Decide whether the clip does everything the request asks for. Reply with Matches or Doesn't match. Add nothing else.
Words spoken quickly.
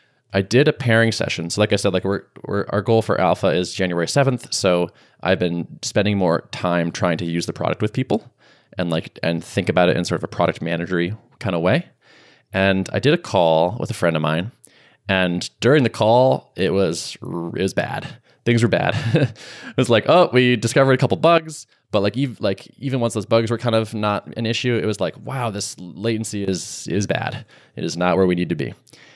Matches